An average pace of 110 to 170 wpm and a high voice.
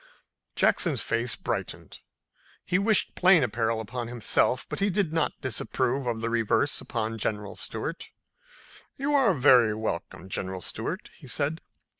No: average, 140 wpm; low, 120 Hz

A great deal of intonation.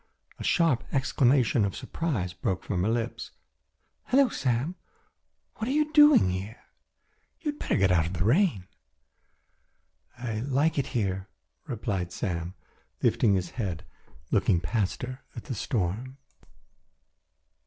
Yes: wide, 6.8 semitones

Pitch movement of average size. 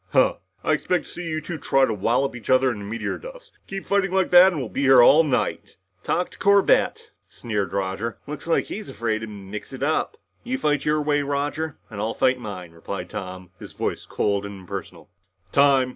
No: wide, 7.1 semitones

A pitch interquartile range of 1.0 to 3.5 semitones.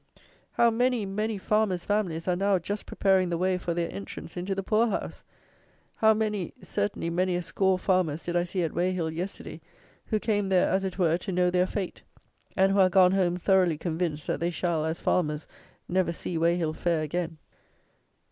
Yes: narrow, 2.4 semitones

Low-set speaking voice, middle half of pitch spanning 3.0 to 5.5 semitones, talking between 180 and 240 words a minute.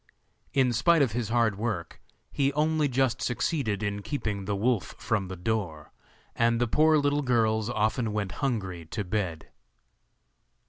No: low, 115 Hz; average, 4.3 semitones; average, 150 wpm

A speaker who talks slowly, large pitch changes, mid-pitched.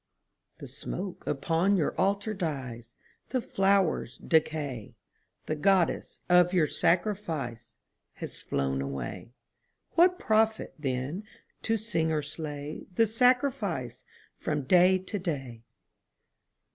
Yes: slow, 110 wpm; wide, 6.6 semitones; medium, 165 Hz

